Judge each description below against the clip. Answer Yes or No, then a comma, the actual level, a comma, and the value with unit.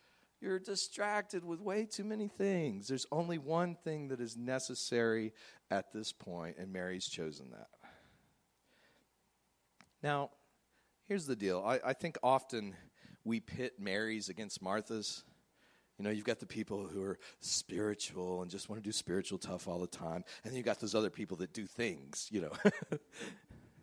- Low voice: Yes, low, 115 Hz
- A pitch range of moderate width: No, wide, 8.7 semitones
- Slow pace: No, average, 165 wpm